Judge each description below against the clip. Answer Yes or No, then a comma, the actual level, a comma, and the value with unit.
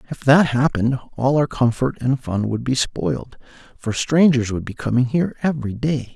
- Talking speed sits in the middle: Yes, average, 185 wpm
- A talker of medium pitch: No, low, 130 Hz